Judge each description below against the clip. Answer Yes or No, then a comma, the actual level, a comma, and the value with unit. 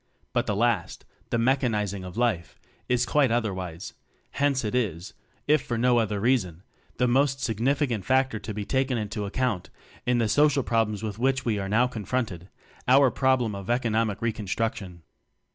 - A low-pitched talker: Yes, low, 115 Hz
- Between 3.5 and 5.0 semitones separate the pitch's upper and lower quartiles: Yes, average, 3.8 semitones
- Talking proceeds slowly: No, average, 165 wpm